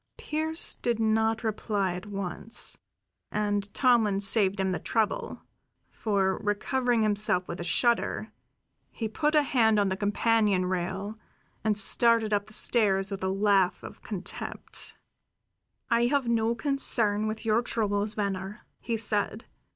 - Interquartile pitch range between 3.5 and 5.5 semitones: No, narrow, 2.5 semitones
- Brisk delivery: No, average, 140 wpm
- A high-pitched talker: Yes, high, 215 Hz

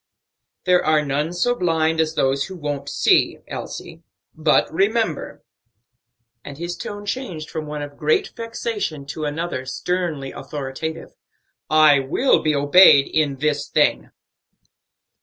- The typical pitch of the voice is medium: Yes, medium, 155 Hz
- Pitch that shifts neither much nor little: Yes, average, 3.6 semitones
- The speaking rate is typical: No, slow, 130 wpm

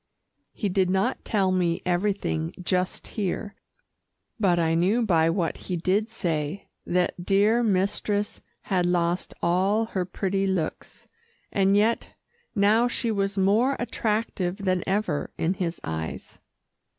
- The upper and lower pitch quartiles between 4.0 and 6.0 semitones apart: No, average, 2.8 semitones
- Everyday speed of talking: No, slow, 130 wpm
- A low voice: No, high, 190 Hz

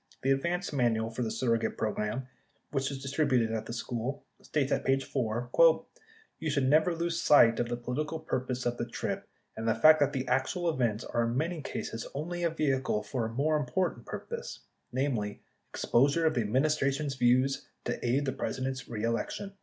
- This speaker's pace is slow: No, average, 195 wpm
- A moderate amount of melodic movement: Yes, average, 4.4 semitones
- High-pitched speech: No, low, 135 Hz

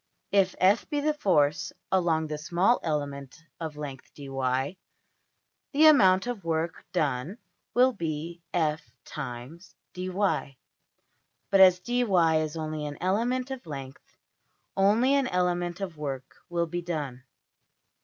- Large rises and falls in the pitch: No, average, 4.6 semitones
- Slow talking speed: Yes, slow, 130 wpm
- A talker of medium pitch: Yes, medium, 170 Hz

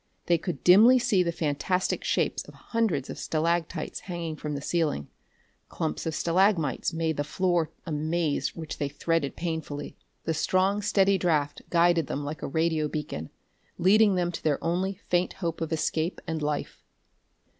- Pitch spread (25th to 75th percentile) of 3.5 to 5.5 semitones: No, average, 3.0 semitones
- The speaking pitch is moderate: Yes, medium, 165 Hz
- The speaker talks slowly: No, average, 165 wpm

